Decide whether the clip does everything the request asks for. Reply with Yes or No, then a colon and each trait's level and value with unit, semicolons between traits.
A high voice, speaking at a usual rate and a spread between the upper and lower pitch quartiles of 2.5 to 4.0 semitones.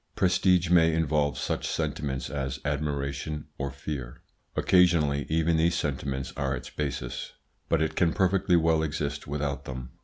No: very low, 75 Hz; average, 145 wpm; average, 2.8 semitones